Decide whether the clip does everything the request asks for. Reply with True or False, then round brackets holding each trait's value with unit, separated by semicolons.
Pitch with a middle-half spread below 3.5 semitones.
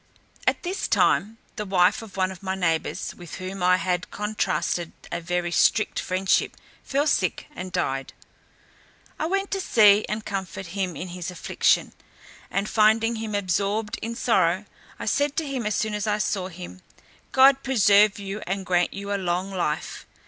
True (3.0 semitones)